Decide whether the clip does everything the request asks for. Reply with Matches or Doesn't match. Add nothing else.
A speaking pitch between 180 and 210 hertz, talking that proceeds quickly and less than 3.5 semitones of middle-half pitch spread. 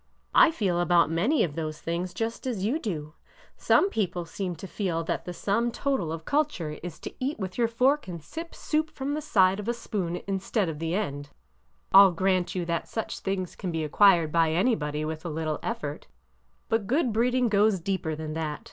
Doesn't match